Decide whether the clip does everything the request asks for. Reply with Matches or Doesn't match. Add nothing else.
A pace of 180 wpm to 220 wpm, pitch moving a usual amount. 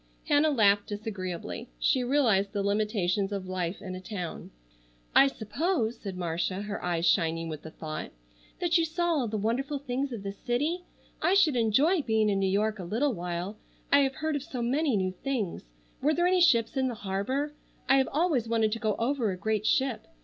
Doesn't match